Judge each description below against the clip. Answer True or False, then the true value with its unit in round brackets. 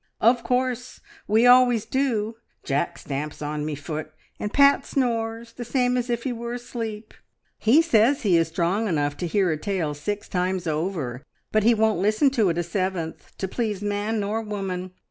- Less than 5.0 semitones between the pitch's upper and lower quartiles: False (5.3 semitones)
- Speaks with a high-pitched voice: True (210 Hz)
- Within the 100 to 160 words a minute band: False (185 wpm)